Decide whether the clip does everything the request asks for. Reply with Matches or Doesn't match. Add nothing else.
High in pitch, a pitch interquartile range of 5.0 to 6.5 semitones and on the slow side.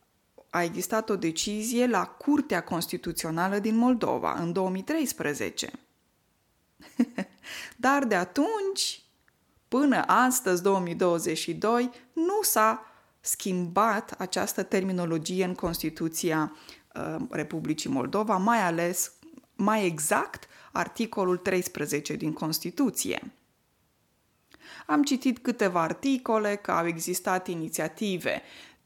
Matches